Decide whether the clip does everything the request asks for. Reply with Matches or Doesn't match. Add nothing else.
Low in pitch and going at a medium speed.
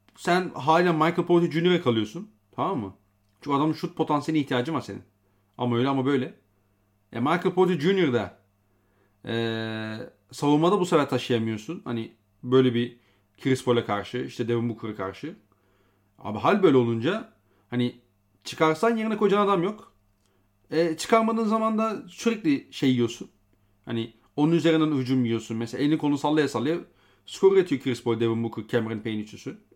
Doesn't match